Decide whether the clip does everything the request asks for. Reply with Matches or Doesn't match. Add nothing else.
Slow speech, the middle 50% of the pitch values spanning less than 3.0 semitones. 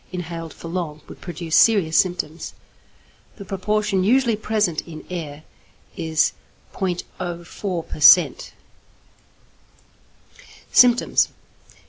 Doesn't match